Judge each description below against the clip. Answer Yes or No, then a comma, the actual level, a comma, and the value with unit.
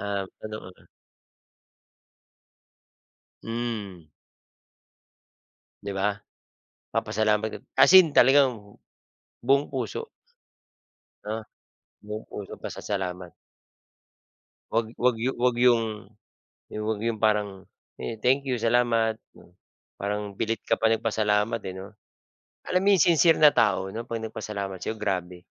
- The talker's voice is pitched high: No, low, 110 Hz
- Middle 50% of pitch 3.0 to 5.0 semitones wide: No, narrow, 2.6 semitones